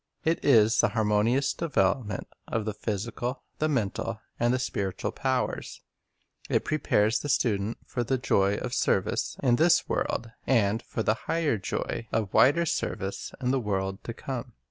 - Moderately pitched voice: No, low, 115 Hz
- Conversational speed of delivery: Yes, average, 165 wpm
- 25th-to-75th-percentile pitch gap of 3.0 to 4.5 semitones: Yes, average, 4.0 semitones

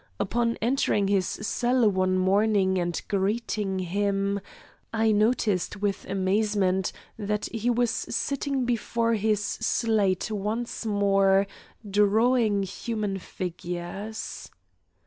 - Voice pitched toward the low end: No, high, 205 Hz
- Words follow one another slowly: Yes, slow, 100 wpm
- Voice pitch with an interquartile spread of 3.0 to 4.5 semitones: No, narrow, 2.6 semitones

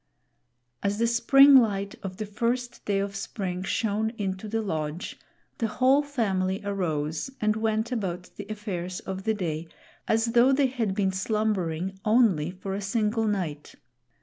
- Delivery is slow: No, average, 155 wpm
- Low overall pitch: No, high, 205 Hz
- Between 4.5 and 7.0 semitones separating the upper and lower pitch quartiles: No, average, 3.2 semitones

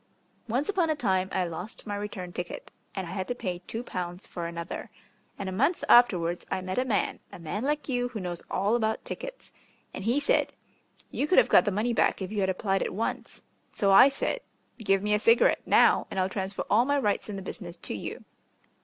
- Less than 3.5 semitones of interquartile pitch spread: No, average, 4.7 semitones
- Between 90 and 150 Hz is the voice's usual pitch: No, high, 205 Hz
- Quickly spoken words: Yes, fast, 225 wpm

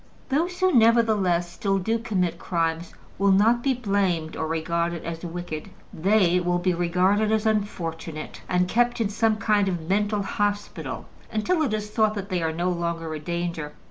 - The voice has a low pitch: No, high, 190 Hz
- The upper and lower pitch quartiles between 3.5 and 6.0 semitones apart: Yes, average, 4.1 semitones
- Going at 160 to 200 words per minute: Yes, average, 175 wpm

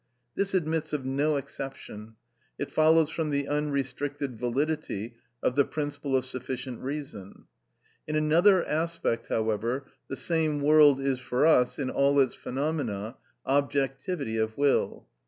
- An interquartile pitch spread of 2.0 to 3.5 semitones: Yes, average, 3.1 semitones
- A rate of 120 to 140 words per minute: Yes, slow, 135 wpm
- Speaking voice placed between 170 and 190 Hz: No, medium, 140 Hz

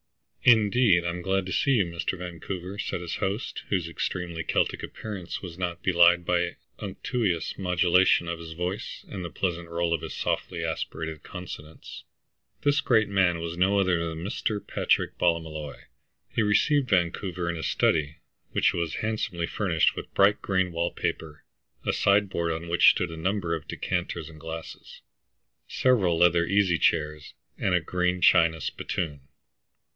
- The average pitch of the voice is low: Yes, very low, 90 Hz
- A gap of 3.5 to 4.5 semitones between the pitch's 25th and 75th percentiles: No, narrow, 2.5 semitones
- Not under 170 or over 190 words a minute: No, average, 155 wpm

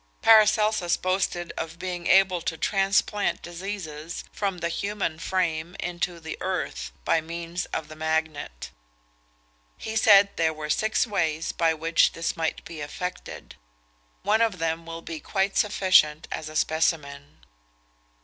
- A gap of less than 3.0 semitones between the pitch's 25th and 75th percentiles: No, average, 3.4 semitones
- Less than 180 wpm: Yes, average, 140 wpm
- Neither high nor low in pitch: Yes, medium, 170 Hz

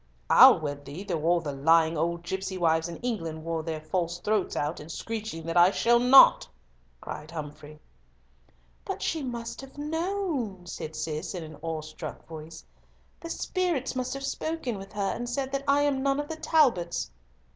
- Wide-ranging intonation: Yes, wide, 8.7 semitones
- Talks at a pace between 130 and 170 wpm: No, average, 180 wpm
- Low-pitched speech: No, medium, 185 Hz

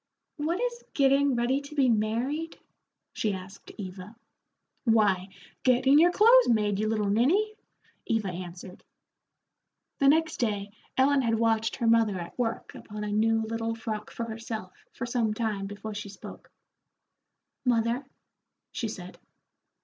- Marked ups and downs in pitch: No, average, 4.1 semitones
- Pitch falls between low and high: No, high, 225 Hz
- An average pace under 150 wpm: Yes, average, 140 wpm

